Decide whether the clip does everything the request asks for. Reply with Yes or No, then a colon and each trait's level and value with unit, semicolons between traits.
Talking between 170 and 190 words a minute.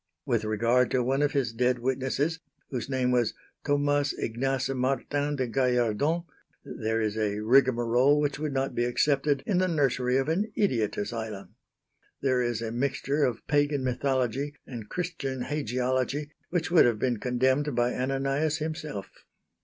No: average, 155 wpm